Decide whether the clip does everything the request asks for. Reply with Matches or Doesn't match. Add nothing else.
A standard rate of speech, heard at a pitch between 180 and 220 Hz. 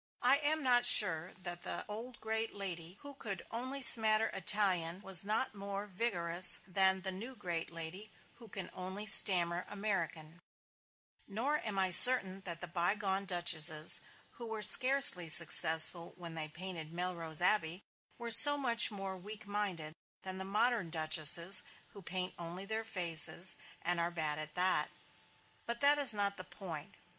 Matches